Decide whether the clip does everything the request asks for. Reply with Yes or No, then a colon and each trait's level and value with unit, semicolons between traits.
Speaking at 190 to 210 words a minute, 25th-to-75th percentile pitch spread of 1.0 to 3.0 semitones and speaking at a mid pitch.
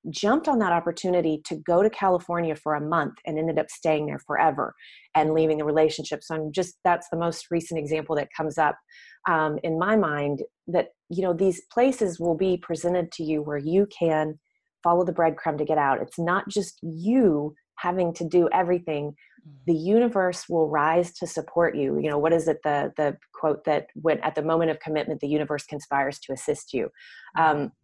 Yes: average, 200 wpm; narrow, 2.4 semitones; medium, 165 Hz